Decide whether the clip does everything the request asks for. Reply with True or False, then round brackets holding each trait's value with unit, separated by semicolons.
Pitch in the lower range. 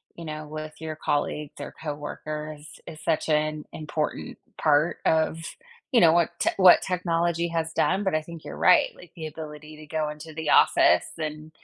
False (155 Hz)